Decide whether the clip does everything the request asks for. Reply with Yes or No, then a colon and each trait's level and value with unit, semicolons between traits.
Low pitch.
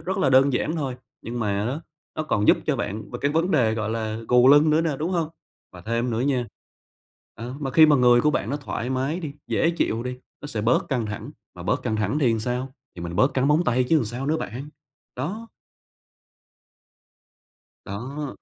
Yes: low, 130 Hz